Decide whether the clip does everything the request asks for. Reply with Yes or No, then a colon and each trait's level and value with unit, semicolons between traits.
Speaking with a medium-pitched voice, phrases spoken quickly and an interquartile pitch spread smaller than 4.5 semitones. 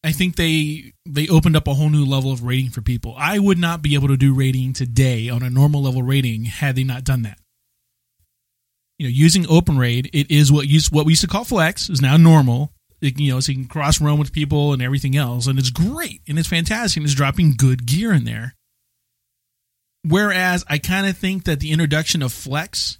Yes: medium, 145 Hz; fast, 225 wpm; average, 3.8 semitones